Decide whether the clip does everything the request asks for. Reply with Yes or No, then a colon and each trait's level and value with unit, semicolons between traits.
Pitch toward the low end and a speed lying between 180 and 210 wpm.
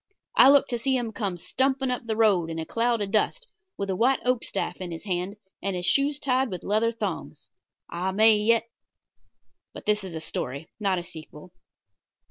No: high, 210 Hz; average, 200 wpm